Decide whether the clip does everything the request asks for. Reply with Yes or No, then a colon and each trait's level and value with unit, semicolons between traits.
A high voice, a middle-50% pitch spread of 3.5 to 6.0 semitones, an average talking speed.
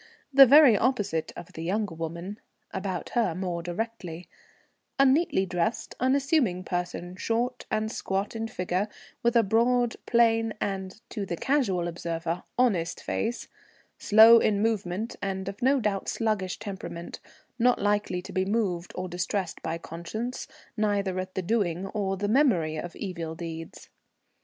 Yes: high, 195 Hz; average, 4.3 semitones; average, 145 wpm